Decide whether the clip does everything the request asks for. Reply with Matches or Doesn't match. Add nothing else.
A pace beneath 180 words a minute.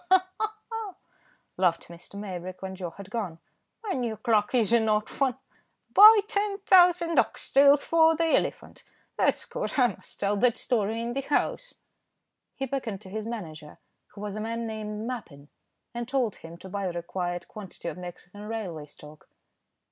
Matches